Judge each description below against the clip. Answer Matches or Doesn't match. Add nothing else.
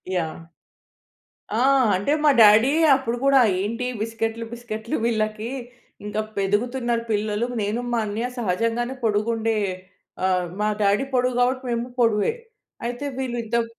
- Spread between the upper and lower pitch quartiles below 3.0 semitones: Matches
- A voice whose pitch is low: Doesn't match